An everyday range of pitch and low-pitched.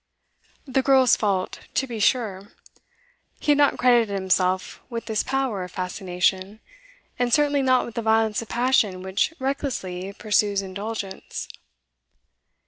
No: average, 5.0 semitones; high, 220 Hz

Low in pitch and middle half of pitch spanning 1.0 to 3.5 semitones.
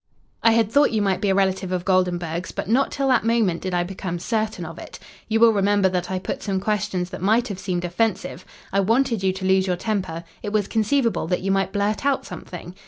No: high, 195 Hz; average, 3.2 semitones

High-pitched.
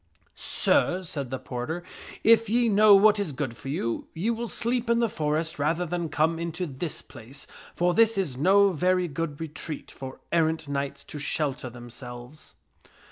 No: medium, 160 Hz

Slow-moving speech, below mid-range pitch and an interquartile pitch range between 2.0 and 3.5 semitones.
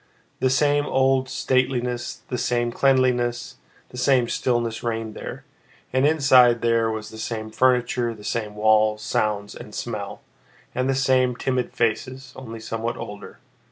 No: average, 145 wpm; low, 120 Hz; narrow, 2.5 semitones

